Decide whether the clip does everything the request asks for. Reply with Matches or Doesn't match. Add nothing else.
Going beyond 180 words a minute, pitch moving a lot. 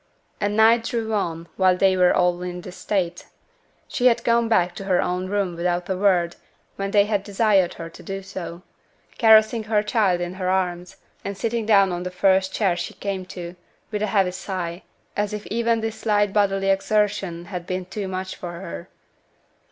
Doesn't match